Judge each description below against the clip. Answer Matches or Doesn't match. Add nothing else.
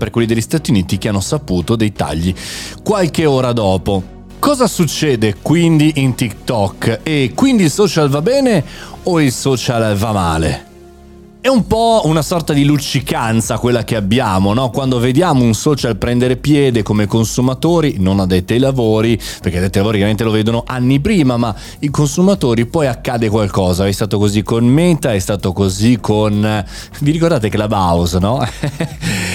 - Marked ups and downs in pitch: Matches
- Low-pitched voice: Matches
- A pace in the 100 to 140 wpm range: Doesn't match